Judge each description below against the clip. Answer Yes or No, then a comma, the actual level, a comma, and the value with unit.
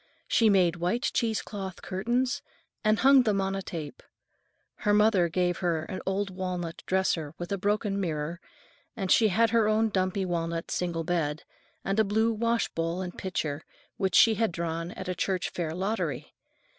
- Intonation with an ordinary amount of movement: Yes, average, 3.8 semitones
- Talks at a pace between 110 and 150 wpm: No, average, 170 wpm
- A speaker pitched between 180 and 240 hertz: Yes, high, 190 Hz